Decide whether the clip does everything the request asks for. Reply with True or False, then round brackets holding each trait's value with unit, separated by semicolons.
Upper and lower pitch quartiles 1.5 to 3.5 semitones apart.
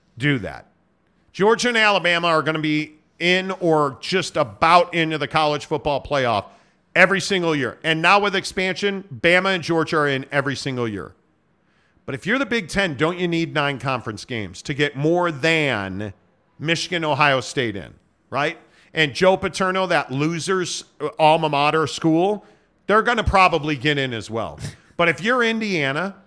False (4.3 semitones)